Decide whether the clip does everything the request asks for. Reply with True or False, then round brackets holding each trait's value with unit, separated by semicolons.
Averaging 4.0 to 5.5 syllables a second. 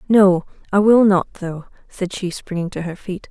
True (4.5 syllables/s)